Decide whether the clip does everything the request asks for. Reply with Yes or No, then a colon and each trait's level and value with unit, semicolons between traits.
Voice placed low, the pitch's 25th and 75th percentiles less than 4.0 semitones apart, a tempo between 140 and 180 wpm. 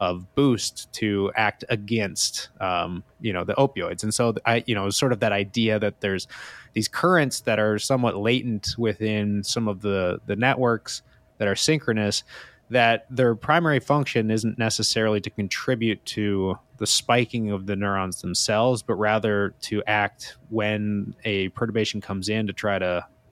Yes: low, 110 Hz; average, 2.7 semitones; average, 160 wpm